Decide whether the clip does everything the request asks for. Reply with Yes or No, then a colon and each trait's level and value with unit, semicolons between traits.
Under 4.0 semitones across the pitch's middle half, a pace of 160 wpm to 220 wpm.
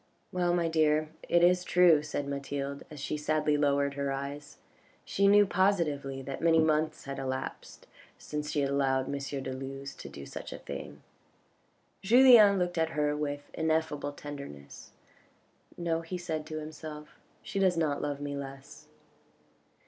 Yes: average, 2.8 semitones; average, 165 wpm